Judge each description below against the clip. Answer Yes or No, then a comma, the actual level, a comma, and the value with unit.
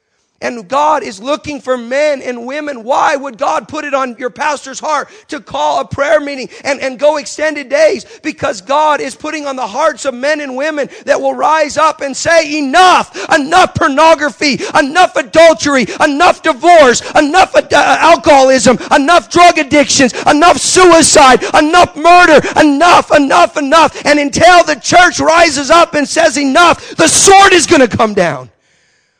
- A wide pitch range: No, average, 2.8 semitones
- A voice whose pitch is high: Yes, very high, 300 Hz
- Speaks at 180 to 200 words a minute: No, average, 165 wpm